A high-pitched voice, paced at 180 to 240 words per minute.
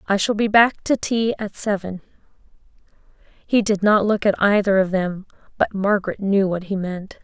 Yes: high, 200 Hz; average, 185 wpm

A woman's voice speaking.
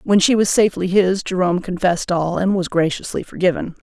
Yes: female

